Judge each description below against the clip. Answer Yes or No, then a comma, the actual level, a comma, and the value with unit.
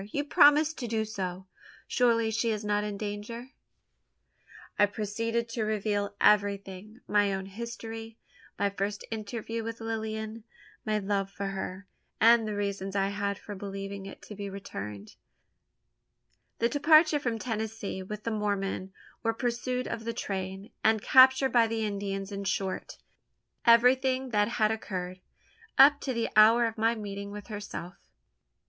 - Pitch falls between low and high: No, high, 215 Hz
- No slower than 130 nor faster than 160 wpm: Yes, average, 150 wpm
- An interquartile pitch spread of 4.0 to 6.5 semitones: No, narrow, 2.5 semitones